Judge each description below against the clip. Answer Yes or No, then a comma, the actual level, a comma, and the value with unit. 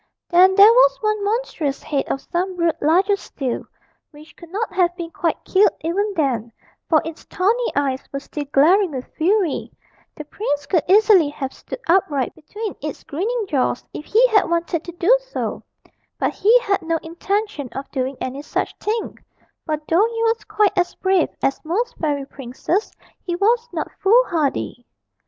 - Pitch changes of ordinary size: No, wide, 6.0 semitones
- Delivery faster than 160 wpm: Yes, average, 170 wpm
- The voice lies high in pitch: Yes, very high, 345 Hz